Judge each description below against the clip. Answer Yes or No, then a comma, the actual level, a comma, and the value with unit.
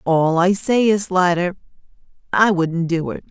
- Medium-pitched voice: Yes, medium, 180 Hz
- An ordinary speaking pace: Yes, average, 165 wpm